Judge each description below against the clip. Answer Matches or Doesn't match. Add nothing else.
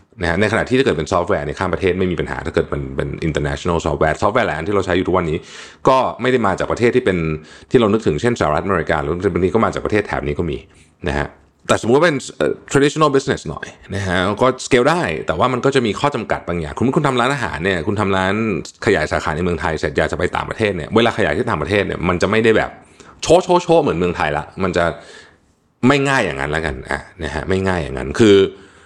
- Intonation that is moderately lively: Doesn't match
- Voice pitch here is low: Matches